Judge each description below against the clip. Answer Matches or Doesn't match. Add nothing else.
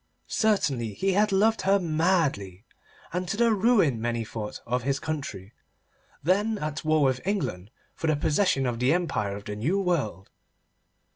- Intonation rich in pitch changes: Matches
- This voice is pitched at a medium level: Matches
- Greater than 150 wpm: Matches